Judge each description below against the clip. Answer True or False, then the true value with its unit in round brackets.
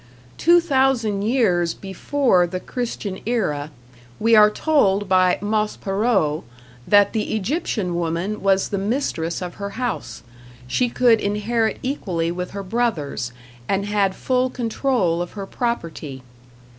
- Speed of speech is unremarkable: False (130 wpm)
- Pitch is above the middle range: True (205 Hz)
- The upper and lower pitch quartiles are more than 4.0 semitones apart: True (4.9 semitones)